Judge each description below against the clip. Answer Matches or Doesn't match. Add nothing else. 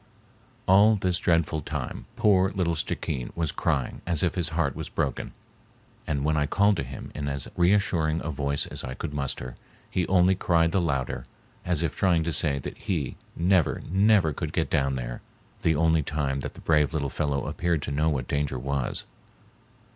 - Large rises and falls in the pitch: Doesn't match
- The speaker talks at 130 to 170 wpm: Doesn't match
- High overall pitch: Doesn't match